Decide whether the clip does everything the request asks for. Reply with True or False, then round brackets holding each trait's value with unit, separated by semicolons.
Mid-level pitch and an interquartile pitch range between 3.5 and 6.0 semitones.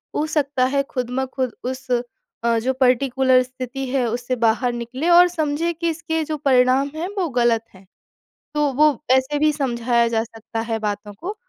False (260 Hz; 3.9 semitones)